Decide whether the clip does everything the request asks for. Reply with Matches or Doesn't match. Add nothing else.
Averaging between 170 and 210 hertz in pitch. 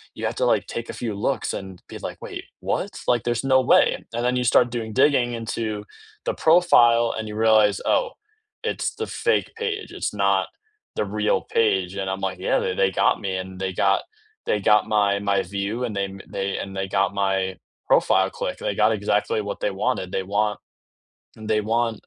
Doesn't match